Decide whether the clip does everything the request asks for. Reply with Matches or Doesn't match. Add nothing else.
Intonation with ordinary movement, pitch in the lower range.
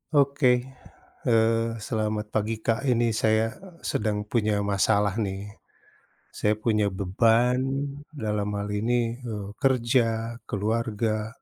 Doesn't match